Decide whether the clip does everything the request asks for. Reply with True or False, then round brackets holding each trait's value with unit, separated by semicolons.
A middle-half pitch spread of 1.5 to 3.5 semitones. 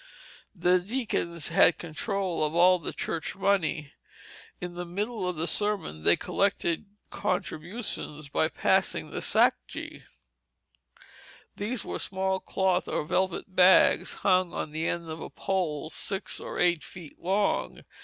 True (2.8 semitones)